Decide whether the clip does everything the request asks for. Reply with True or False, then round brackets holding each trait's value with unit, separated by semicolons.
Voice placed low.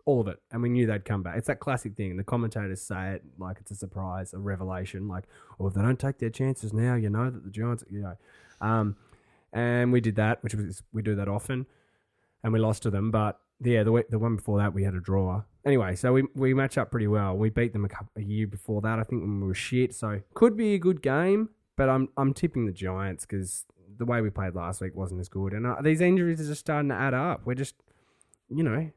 True (110 Hz)